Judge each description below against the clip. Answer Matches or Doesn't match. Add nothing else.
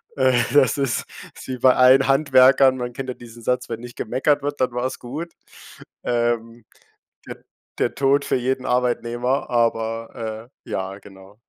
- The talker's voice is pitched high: Doesn't match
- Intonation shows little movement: Matches